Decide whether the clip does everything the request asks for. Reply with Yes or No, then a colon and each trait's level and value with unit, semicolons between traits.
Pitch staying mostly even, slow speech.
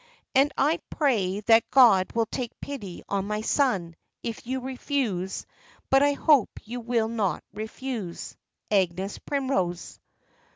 No: wide, 5.4 semitones; slow, 130 wpm